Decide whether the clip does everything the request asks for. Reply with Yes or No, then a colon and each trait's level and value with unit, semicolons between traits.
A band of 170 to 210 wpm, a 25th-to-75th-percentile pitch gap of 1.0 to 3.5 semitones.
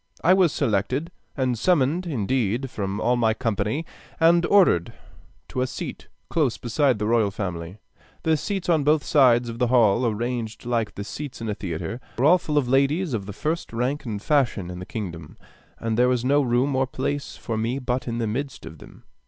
No: average, 200 wpm; average, 4.6 semitones